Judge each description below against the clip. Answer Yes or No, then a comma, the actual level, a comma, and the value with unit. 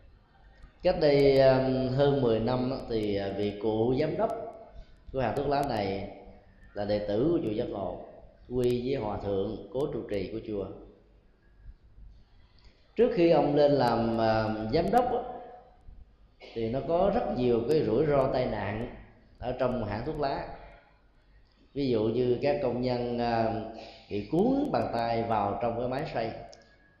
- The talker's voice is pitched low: Yes, low, 120 Hz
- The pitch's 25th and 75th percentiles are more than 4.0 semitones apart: Yes, average, 4.8 semitones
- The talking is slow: Yes, slow, 150 wpm